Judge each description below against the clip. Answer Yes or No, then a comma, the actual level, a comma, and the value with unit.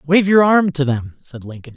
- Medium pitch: Yes, medium, 150 Hz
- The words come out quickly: Yes, fast, 240 wpm